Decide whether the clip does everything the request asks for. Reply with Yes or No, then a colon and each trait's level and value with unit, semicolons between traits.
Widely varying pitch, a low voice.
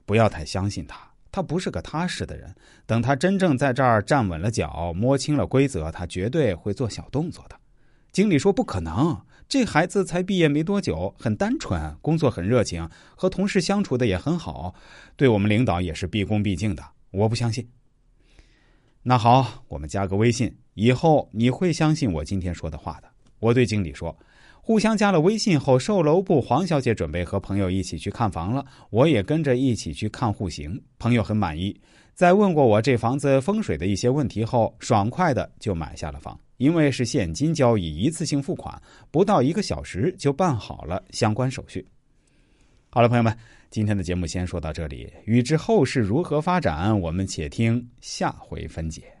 Yes: wide, 6.9 semitones; low, 120 Hz